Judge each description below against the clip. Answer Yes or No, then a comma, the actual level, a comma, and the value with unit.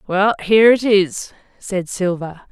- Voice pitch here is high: Yes, high, 195 Hz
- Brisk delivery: No, average, 145 wpm